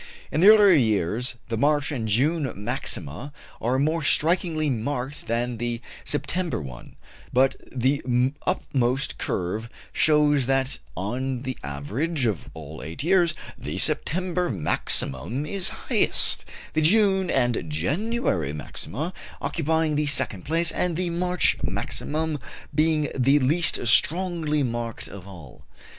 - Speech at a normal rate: No, slow, 130 wpm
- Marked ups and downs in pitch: Yes, wide, 5.8 semitones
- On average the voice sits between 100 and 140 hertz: Yes, low, 135 Hz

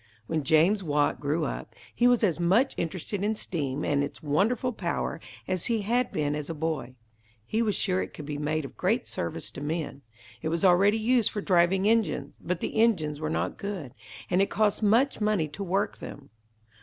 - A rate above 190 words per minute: Yes, average, 200 wpm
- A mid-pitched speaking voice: Yes, medium, 175 Hz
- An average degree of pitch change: No, wide, 5.9 semitones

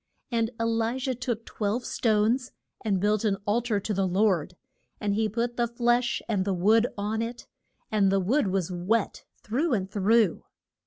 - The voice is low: No, high, 220 Hz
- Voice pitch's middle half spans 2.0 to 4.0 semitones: Yes, average, 3.1 semitones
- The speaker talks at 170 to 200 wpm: Yes, average, 180 wpm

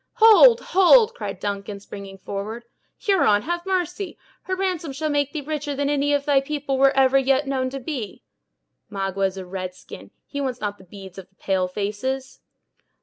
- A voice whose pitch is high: Yes, very high, 270 Hz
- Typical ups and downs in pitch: No, wide, 7.1 semitones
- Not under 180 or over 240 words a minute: Yes, average, 185 wpm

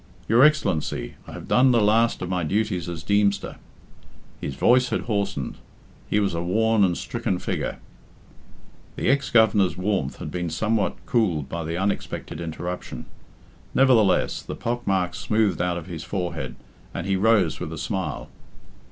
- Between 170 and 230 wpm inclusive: No, average, 160 wpm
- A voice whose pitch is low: Yes, very low, 95 Hz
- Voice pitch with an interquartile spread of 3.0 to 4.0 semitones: No, average, 4.7 semitones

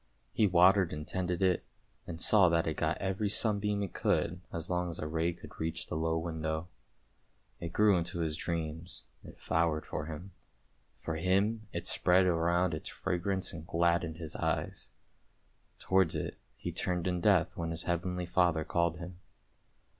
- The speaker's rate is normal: Yes, average, 170 wpm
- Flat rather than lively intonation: Yes, narrow, 2.1 semitones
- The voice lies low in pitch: Yes, very low, 85 Hz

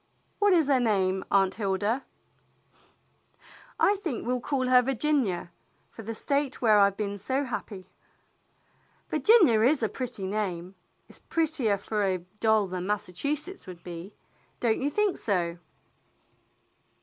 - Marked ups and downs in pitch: Yes, wide, 6.0 semitones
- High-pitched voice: Yes, high, 220 Hz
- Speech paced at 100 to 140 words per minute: Yes, slow, 135 wpm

